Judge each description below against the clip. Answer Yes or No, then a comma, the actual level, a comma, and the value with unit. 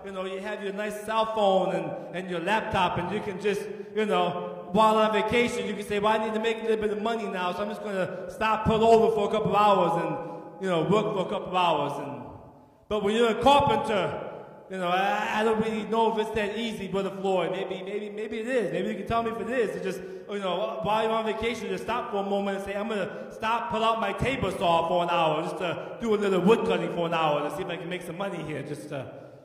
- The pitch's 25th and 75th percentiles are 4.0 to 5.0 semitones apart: No, average, 3.3 semitones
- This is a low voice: No, high, 200 Hz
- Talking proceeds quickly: Yes, fast, 285 wpm